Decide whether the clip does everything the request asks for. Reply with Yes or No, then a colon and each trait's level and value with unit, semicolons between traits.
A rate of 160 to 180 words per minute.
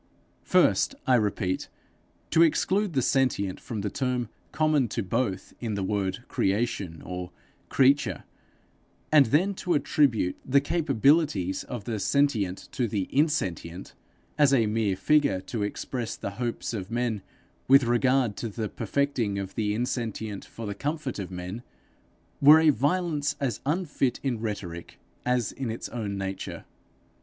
No: average, 145 wpm